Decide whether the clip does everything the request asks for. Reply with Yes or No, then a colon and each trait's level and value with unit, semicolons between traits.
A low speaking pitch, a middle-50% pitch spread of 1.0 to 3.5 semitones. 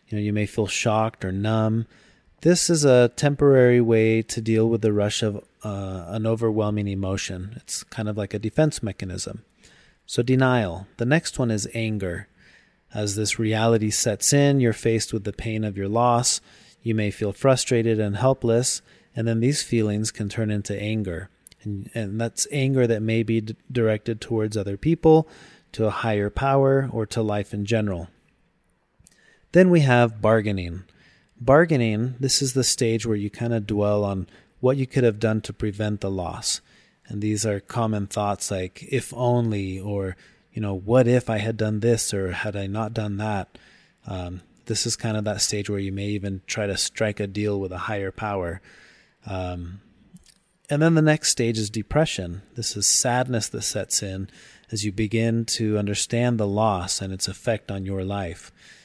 Yes: low, 110 Hz; narrow, 2.6 semitones